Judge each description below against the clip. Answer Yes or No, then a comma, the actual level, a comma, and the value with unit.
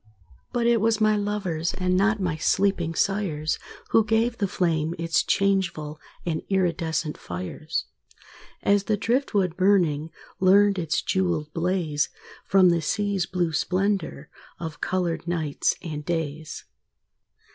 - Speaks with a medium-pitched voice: Yes, medium, 180 Hz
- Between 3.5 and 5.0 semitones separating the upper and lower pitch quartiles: Yes, average, 3.9 semitones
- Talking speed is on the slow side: Yes, slow, 125 wpm